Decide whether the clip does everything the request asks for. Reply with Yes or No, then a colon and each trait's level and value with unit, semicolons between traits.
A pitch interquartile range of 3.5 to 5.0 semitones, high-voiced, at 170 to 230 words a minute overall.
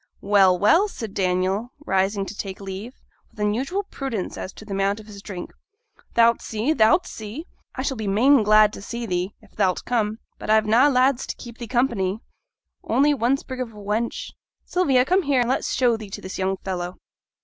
Yes: average, 4.4 semitones; high, 220 Hz; average, 200 wpm